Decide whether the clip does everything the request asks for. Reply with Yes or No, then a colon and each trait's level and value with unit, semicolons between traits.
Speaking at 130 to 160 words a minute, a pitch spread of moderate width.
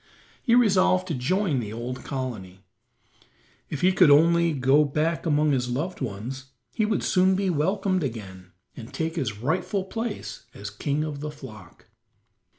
No: average, 155 wpm; wide, 6.7 semitones